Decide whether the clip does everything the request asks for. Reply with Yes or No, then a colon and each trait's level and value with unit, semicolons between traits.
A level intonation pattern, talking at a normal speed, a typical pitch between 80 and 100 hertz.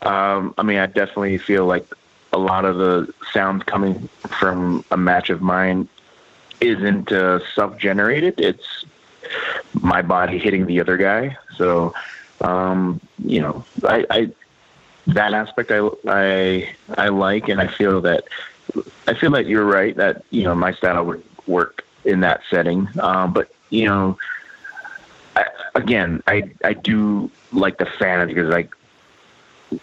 Yes: narrow, 1.9 semitones; average, 150 wpm; very low, 95 Hz